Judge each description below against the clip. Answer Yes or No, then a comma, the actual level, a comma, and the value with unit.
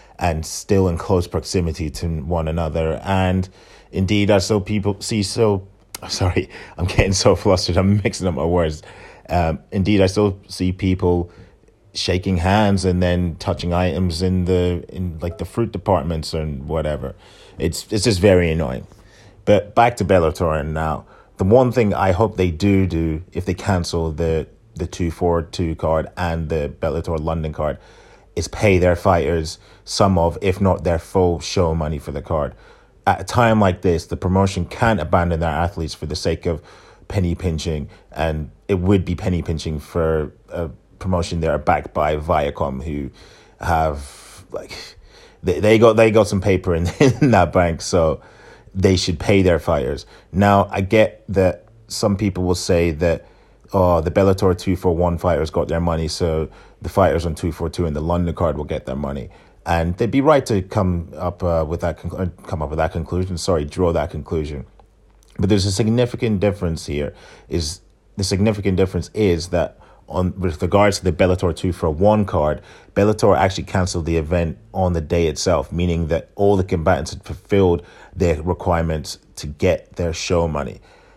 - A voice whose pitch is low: Yes, very low, 90 Hz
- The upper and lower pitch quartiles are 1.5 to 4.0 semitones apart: Yes, average, 2.9 semitones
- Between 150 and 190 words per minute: Yes, average, 180 wpm